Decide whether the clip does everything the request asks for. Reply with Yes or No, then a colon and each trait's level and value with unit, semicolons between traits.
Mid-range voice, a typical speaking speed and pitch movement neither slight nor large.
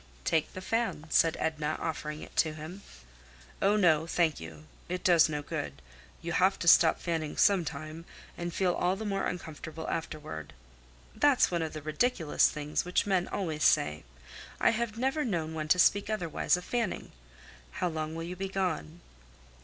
Yes: medium, 165 Hz; average, 175 wpm; average, 3.5 semitones